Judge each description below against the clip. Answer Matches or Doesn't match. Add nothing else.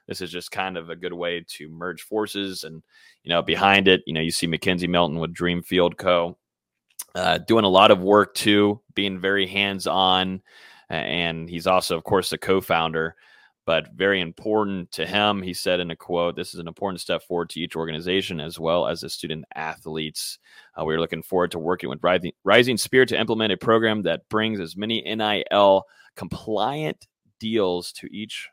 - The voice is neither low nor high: Doesn't match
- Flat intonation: Doesn't match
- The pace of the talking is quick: Doesn't match